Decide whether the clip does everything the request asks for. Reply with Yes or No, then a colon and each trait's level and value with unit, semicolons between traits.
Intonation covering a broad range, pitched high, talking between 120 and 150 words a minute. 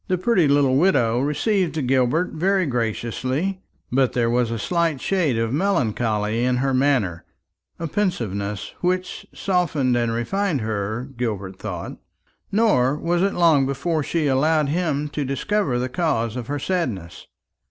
No: wide, 6.4 semitones; low, 135 Hz; average, 145 wpm